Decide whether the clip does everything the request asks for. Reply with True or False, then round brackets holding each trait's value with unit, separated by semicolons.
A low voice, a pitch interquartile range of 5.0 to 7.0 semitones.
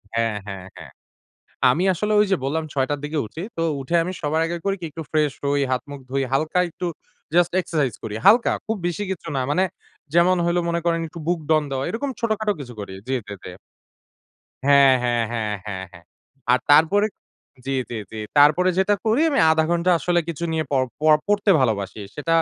False (155 Hz; 5.3 semitones)